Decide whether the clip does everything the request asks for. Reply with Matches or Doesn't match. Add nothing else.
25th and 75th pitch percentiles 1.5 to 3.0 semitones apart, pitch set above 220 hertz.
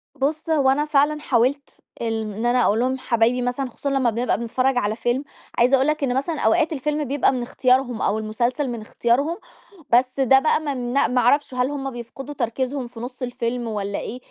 Matches